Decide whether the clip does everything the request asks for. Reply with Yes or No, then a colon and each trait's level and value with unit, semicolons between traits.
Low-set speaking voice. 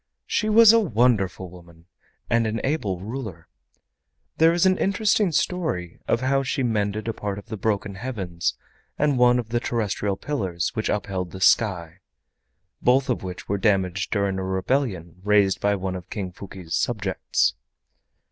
Yes: low, 105 Hz